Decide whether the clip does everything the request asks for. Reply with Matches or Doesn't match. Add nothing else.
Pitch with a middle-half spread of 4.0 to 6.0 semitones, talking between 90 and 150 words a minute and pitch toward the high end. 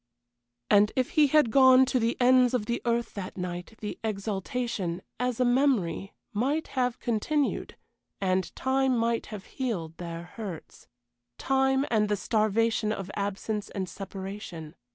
Matches